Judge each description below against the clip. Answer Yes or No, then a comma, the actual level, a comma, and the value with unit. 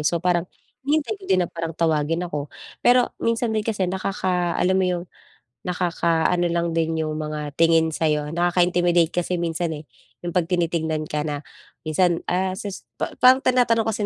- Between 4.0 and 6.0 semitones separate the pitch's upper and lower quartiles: No, narrow, 2.5 semitones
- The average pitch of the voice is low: No, medium, 175 Hz